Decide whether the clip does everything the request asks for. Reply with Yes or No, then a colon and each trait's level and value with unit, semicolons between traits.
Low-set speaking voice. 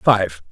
Yes: very low, 95 Hz